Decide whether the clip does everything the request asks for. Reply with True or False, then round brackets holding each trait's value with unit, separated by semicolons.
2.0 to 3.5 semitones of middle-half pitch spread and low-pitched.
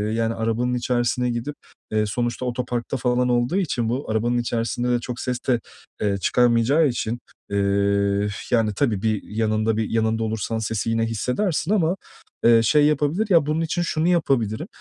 True (2.9 semitones; 120 Hz)